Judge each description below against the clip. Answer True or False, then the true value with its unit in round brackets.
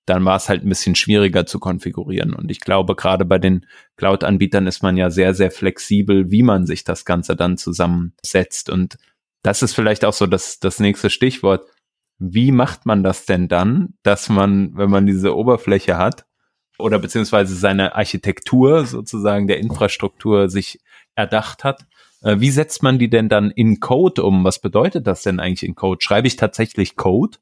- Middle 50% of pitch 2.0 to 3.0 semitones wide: True (2.5 semitones)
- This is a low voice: True (100 Hz)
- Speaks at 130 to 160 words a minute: False (180 wpm)